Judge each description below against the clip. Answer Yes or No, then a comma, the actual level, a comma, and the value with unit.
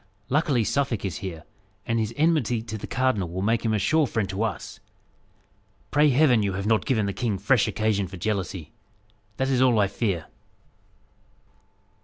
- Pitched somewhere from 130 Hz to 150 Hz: No, low, 110 Hz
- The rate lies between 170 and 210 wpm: Yes, average, 175 wpm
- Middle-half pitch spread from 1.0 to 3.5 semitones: No, average, 4.6 semitones